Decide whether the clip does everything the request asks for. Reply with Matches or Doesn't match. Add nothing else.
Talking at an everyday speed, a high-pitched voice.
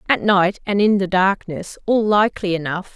Matches